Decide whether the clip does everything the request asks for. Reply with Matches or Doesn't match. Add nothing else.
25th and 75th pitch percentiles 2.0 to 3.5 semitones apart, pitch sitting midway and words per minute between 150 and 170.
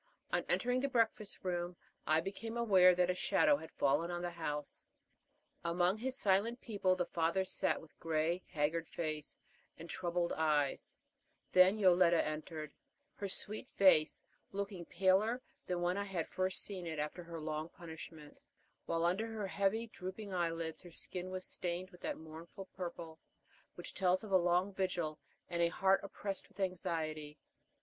Matches